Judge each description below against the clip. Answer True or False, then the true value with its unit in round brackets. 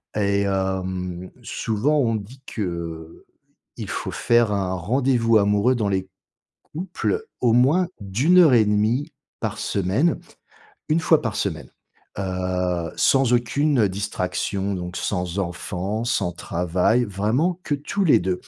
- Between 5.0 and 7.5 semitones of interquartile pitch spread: True (5.5 semitones)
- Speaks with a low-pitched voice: True (105 Hz)